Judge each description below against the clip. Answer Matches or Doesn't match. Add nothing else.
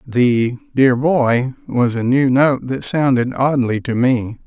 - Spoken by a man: Matches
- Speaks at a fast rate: Doesn't match